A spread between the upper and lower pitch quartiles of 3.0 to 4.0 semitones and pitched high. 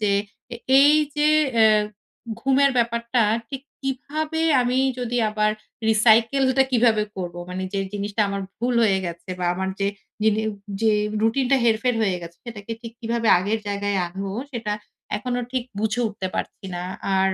Yes: average, 3.4 semitones; high, 220 Hz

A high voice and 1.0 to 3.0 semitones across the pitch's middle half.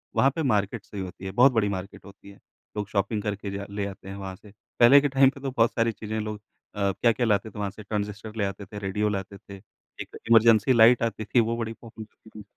No: low, 105 Hz; narrow, 2.5 semitones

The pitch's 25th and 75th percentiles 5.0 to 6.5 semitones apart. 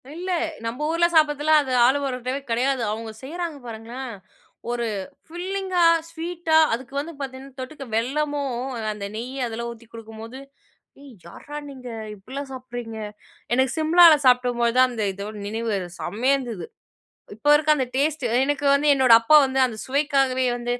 No: average, 3.8 semitones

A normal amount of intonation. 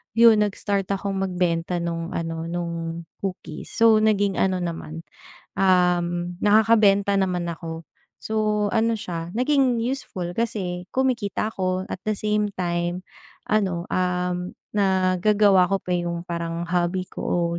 Yes: average, 3.4 semitones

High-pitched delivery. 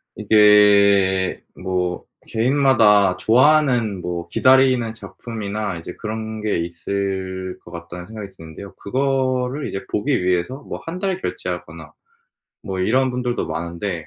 No: low, 105 Hz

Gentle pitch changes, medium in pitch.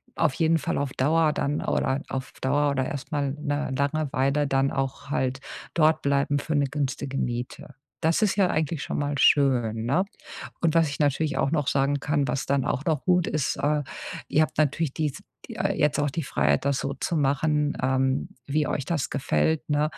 Yes: narrow, 2.2 semitones; medium, 145 Hz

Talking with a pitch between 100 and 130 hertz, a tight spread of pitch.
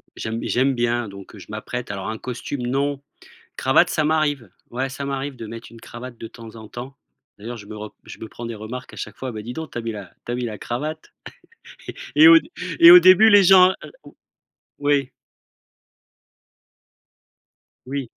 No: low, 125 Hz; average, 4.1 semitones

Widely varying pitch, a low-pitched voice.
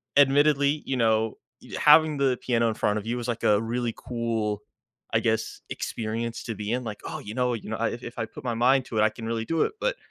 No: narrow, 2.6 semitones; low, 115 Hz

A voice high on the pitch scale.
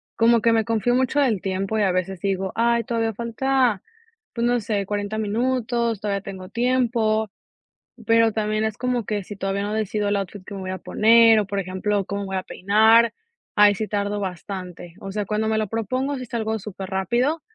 Yes: high, 215 Hz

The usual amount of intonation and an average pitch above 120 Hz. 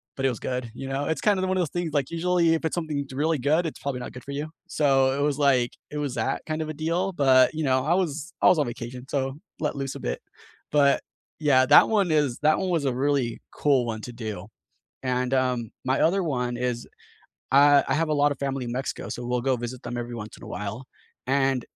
Yes: average, 3.6 semitones; low, 135 Hz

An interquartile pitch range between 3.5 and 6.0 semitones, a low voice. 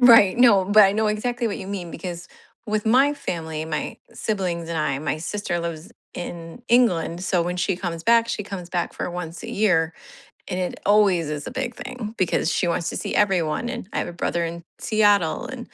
No: average, 4.0 semitones; medium, 185 Hz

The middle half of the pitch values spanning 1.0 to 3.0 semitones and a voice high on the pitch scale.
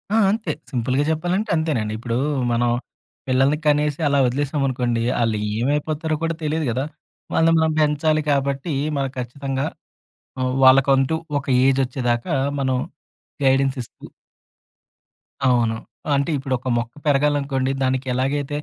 No: narrow, 2.5 semitones; low, 135 Hz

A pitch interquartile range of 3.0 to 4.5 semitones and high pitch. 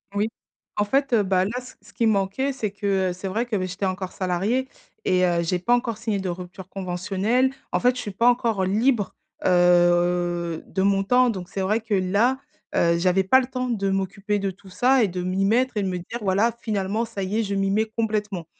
Yes: average, 3.6 semitones; high, 200 Hz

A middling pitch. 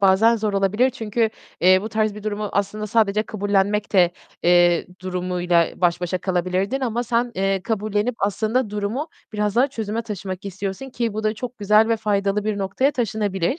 No: high, 210 Hz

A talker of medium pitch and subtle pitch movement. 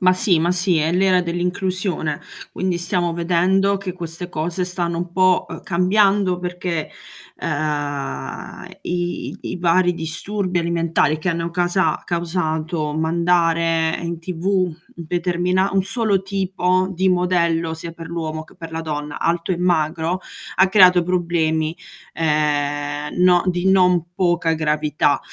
Yes: medium, 175 Hz; narrow, 2.2 semitones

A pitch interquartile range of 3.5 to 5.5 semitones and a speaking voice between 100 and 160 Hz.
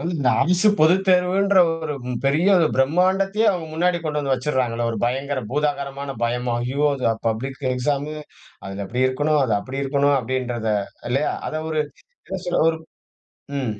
Yes: average, 4.3 semitones; medium, 140 Hz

